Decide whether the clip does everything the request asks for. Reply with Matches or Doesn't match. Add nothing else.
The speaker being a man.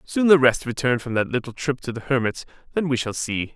Matches